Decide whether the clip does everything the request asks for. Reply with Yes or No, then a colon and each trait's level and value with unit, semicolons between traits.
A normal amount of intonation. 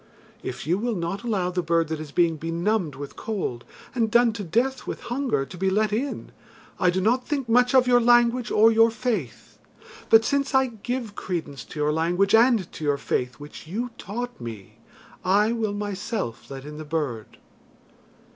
No: wide, 6.6 semitones